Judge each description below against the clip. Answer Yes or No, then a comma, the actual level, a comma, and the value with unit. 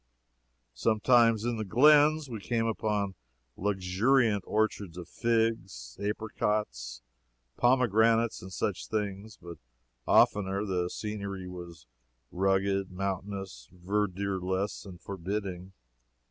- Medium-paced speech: No, slow, 95 wpm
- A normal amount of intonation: Yes, average, 3.1 semitones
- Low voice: Yes, low, 100 Hz